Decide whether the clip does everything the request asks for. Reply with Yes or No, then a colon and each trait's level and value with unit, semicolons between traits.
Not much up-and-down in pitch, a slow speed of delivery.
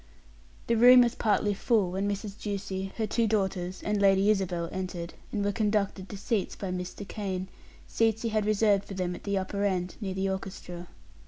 No: narrow, 2.0 semitones; average, 190 wpm